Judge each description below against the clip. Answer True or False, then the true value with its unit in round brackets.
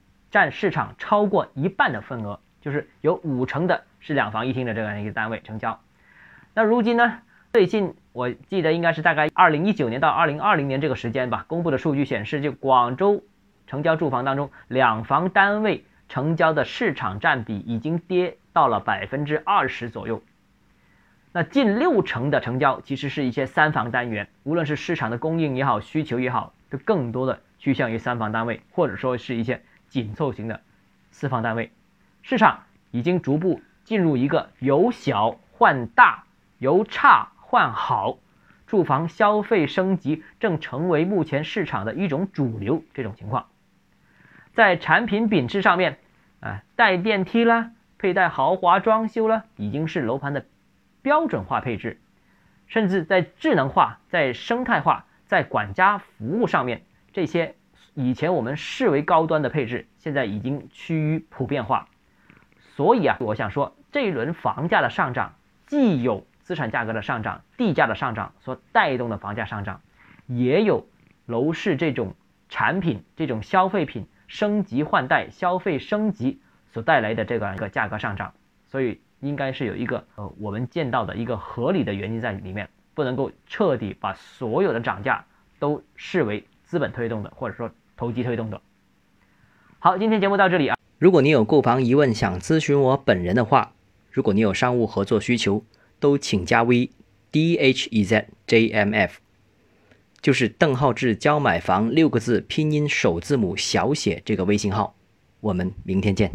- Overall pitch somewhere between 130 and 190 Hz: True (140 Hz)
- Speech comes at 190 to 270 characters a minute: True (260 characters per minute)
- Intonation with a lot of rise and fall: True (7.4 semitones)